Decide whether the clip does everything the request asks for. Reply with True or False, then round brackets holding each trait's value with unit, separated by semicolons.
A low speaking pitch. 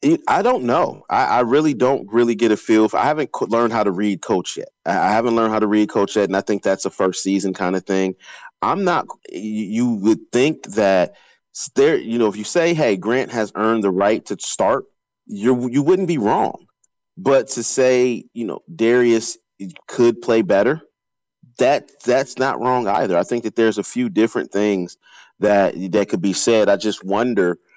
True (110 Hz)